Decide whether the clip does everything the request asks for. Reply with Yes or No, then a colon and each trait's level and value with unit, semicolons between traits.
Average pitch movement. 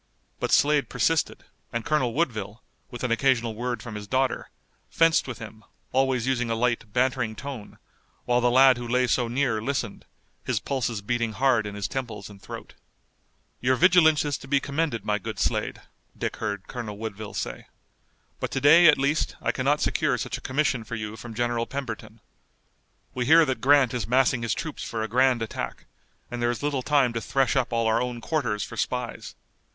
Yes: average, 3.1 semitones